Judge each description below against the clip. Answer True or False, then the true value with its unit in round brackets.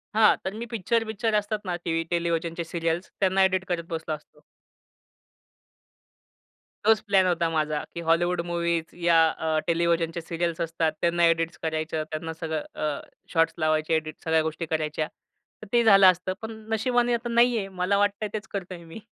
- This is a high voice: False (170 Hz)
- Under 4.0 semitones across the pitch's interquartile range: True (3.4 semitones)